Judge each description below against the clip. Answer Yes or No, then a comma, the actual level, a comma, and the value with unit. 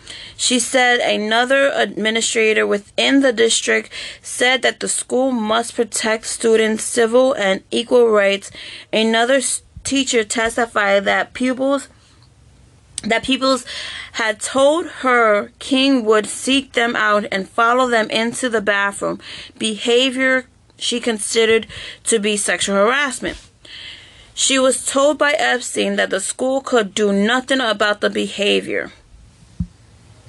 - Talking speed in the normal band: No, slow, 120 wpm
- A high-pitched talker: Yes, high, 230 Hz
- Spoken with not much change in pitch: No, average, 3.4 semitones